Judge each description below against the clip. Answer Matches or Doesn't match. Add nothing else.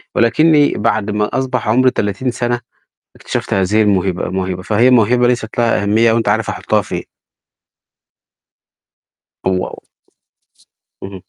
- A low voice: Matches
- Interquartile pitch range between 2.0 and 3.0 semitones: Doesn't match